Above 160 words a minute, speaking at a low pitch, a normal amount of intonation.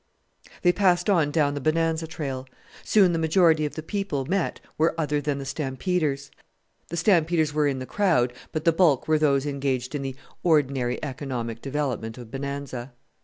No: average, 170 wpm; medium, 150 Hz; average, 3.4 semitones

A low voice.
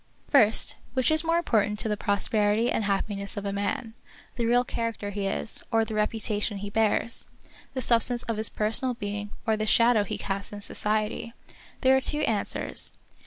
No: high, 215 Hz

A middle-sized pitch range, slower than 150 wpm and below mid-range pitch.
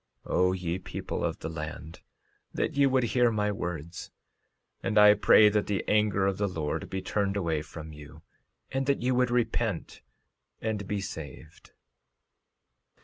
No: average, 4.6 semitones; average, 160 wpm; low, 100 Hz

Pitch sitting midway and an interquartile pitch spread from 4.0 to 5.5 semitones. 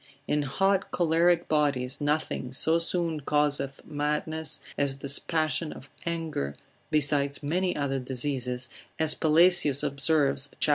No: medium, 150 Hz; narrow, 2.6 semitones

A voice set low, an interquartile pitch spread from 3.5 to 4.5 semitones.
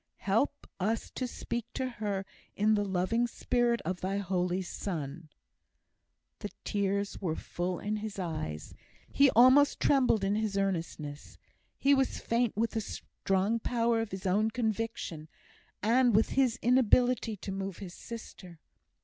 No: high, 210 Hz; average, 3.9 semitones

